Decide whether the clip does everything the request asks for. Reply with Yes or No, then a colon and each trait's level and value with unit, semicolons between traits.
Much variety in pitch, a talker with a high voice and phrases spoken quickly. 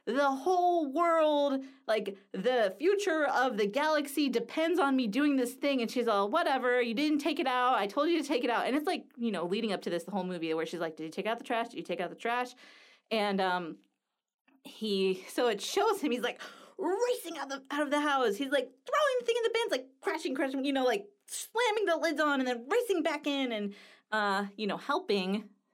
Yes: wide, 6.0 semitones; very high, 270 Hz; fast, 240 wpm